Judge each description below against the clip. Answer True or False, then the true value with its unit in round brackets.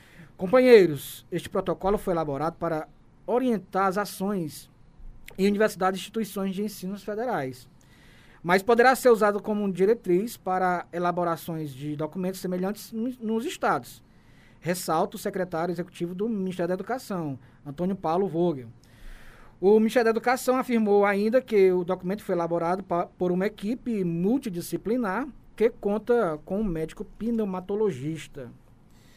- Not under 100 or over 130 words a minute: True (125 wpm)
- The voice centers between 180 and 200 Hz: True (190 Hz)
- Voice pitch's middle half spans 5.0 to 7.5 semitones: False (4.1 semitones)